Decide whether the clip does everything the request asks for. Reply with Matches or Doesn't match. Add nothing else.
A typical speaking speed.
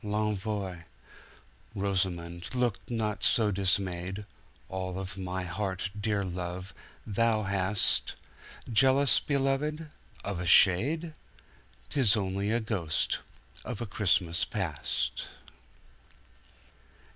Doesn't match